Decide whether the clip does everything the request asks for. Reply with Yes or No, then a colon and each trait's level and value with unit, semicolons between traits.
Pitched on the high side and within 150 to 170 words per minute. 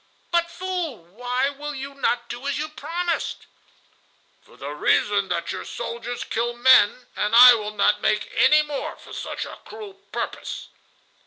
Yes: very high, 250 Hz; average, 160 wpm